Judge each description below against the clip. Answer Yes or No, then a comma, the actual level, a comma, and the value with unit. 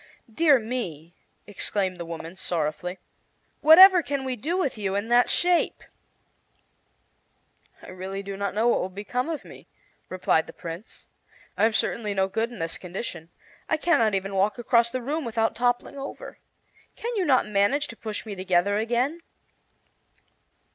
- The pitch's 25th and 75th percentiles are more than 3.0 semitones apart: Yes, average, 5.2 semitones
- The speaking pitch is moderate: No, high, 220 Hz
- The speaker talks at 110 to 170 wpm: Yes, average, 160 wpm